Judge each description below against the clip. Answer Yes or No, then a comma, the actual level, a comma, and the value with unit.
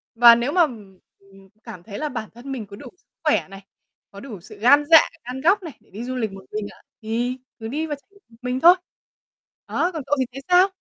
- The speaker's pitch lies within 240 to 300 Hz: Yes, high, 245 Hz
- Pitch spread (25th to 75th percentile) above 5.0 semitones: Yes, wide, 5.4 semitones